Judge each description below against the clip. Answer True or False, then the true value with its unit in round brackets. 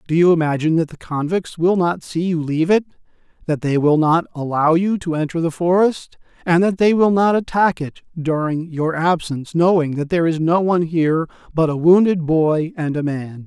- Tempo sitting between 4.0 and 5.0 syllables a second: False (5.3 syllables/s)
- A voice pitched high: False (165 Hz)